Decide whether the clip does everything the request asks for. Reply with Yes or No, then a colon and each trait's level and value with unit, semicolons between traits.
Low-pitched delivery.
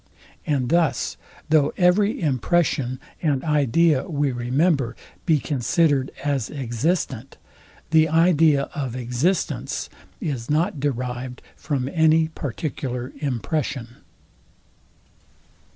No: medium, 145 Hz